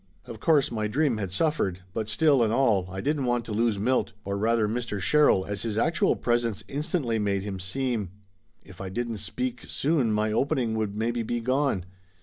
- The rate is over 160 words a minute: Yes, average, 190 wpm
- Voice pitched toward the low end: Yes, low, 115 Hz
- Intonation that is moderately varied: Yes, average, 3.8 semitones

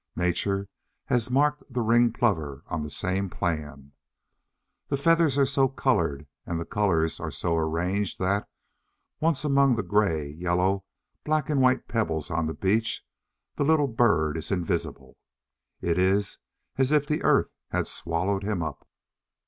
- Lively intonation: Yes, wide, 7.6 semitones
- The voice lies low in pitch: Yes, low, 100 Hz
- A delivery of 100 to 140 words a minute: No, average, 150 wpm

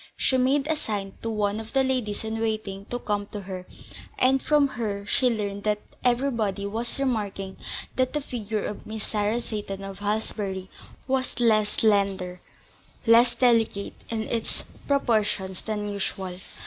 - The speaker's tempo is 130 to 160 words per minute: Yes, average, 155 wpm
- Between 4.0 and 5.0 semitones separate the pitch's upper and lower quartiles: No, average, 3.2 semitones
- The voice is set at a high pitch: Yes, high, 215 Hz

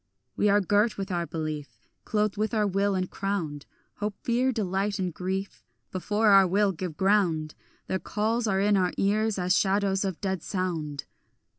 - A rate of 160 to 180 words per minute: Yes, average, 170 wpm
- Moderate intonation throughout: No, narrow, 2.3 semitones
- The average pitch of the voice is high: Yes, high, 195 Hz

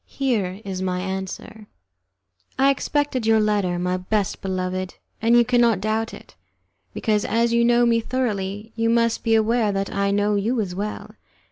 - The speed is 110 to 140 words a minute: No, average, 165 wpm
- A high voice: Yes, high, 215 Hz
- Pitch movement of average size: Yes, average, 3.3 semitones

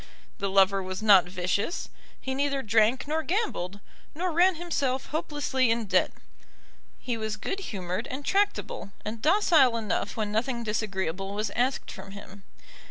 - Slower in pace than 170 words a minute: Yes, average, 150 wpm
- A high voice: Yes, high, 225 Hz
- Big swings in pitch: Yes, wide, 6.3 semitones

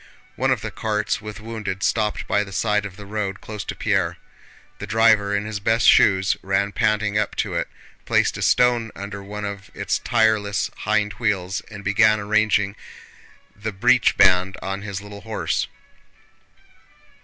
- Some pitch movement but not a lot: No, narrow, 1.5 semitones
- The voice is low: Yes, low, 105 Hz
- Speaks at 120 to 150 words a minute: No, average, 165 wpm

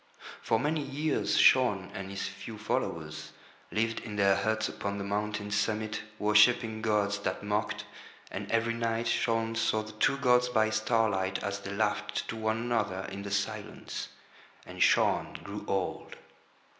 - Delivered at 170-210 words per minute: No, average, 155 wpm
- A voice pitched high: No, low, 110 Hz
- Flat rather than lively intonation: Yes, narrow, 2.1 semitones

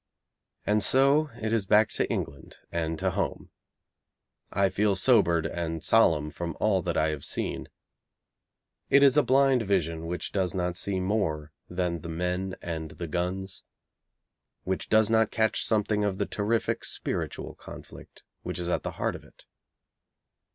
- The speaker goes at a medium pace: Yes, average, 160 wpm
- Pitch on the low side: Yes, very low, 95 Hz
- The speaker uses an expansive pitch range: No, average, 4.4 semitones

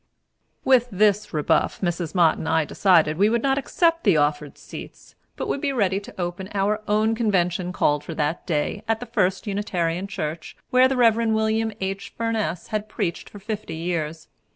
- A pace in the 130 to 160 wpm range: No, average, 185 wpm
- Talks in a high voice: Yes, high, 195 Hz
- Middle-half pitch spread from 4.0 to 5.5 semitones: Yes, average, 4.6 semitones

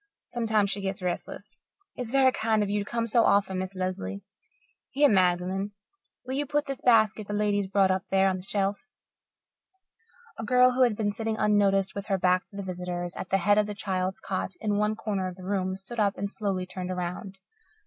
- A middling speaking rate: No, fast, 210 wpm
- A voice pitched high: Yes, high, 200 Hz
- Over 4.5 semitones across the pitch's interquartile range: No, narrow, 2.5 semitones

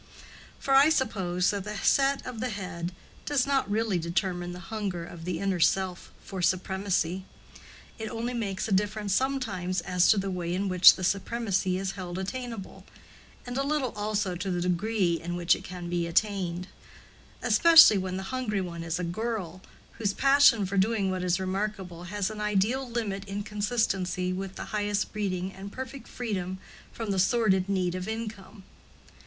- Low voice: No, high, 195 Hz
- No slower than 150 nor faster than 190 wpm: Yes, average, 175 wpm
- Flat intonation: No, average, 3.3 semitones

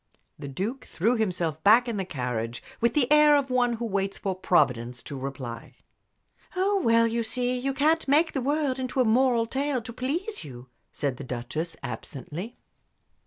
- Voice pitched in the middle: No, high, 230 Hz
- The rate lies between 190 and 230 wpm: No, average, 175 wpm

